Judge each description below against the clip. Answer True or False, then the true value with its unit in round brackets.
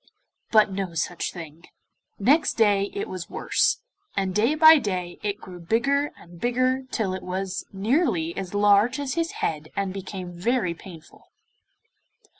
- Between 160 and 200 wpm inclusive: False (150 wpm)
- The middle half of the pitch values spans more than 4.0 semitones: True (5.1 semitones)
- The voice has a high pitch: True (200 Hz)